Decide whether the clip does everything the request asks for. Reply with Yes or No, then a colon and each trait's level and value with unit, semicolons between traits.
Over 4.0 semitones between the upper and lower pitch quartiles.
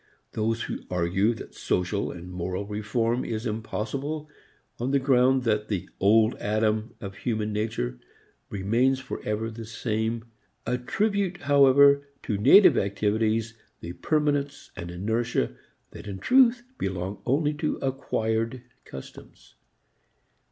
Yes: average, 4.4 semitones